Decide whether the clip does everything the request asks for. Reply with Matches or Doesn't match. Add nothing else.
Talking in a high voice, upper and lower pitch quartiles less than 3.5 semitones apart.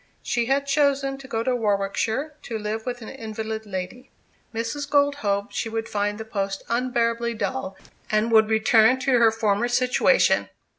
Matches